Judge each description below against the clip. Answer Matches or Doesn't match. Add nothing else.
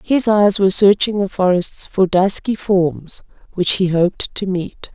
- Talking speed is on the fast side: Doesn't match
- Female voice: Matches